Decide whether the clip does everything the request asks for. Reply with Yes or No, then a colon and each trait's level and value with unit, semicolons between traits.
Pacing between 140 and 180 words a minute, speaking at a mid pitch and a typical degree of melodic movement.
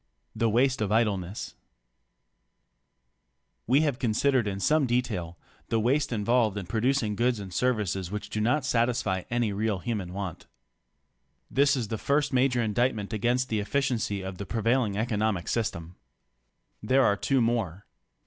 No: average, 145 wpm; low, 115 Hz; average, 3.7 semitones